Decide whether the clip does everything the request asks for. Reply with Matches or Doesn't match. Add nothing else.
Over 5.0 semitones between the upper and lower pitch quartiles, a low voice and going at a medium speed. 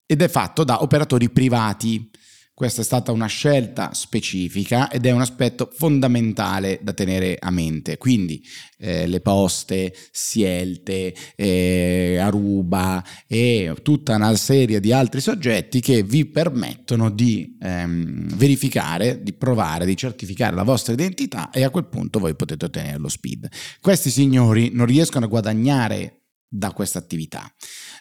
Matches